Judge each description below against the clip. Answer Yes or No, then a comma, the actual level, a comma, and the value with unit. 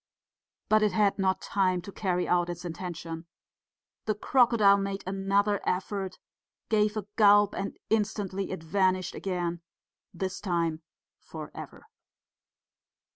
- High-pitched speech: Yes, high, 195 Hz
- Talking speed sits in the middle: No, slow, 125 wpm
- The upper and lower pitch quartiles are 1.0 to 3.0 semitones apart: Yes, narrow, 2.4 semitones